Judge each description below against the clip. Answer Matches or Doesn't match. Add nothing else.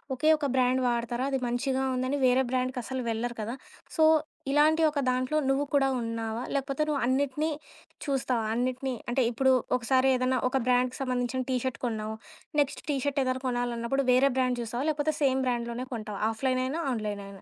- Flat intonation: Matches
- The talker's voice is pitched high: Matches